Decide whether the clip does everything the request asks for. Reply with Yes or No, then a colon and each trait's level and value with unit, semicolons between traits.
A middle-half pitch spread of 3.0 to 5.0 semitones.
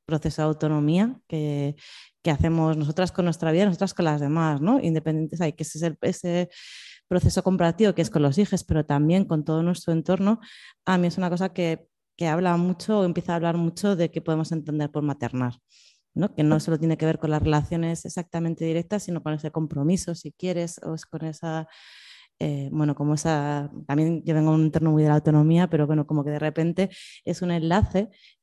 No: narrow, 2.5 semitones